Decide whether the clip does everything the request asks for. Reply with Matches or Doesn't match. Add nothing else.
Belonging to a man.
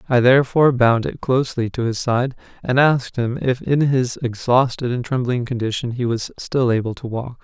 Matches